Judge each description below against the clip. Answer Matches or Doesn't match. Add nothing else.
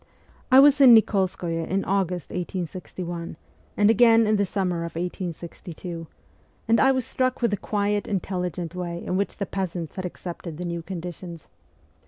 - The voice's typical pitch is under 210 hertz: Matches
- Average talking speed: Matches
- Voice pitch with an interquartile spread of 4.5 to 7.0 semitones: Doesn't match